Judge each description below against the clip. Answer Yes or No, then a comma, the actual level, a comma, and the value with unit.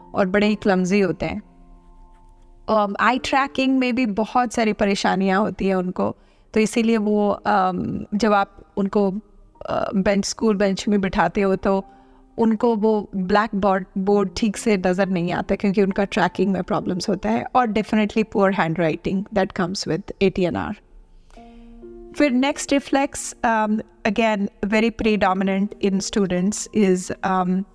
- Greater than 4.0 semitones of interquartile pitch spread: No, narrow, 2.6 semitones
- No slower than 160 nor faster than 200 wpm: No, average, 150 wpm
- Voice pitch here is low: No, high, 205 Hz